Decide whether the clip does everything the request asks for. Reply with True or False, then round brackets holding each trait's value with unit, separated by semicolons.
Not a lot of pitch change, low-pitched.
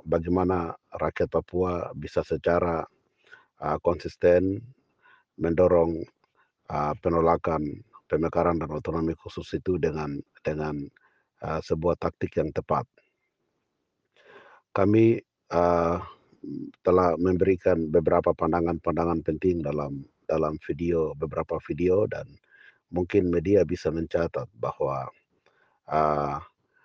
True (2.2 semitones; 85 Hz)